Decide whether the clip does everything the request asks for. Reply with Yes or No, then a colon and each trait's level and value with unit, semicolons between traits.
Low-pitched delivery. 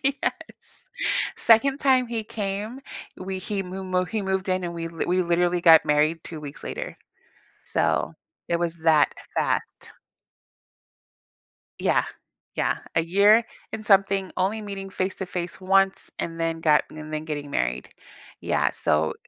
No: medium, 185 Hz